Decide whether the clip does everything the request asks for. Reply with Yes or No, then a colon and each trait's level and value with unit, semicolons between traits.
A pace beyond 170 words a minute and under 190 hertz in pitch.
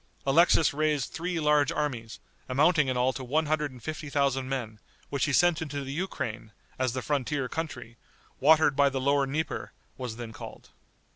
Yes: average, 180 wpm; medium, 140 Hz